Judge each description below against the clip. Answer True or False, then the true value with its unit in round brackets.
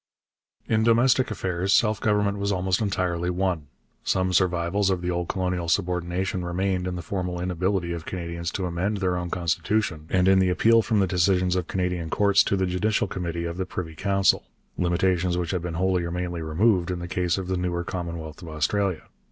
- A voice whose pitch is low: True (90 Hz)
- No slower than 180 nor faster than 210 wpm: True (195 wpm)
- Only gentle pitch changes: True (1.8 semitones)